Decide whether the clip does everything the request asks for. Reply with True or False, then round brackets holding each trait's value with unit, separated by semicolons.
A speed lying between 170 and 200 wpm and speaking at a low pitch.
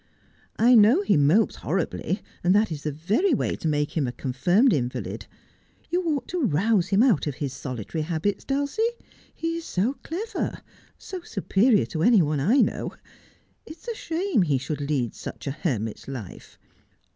False (180 wpm; 185 Hz)